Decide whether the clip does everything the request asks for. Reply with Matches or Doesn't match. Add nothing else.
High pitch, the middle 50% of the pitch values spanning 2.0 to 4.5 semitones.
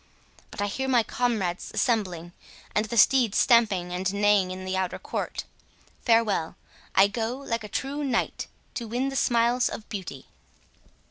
Matches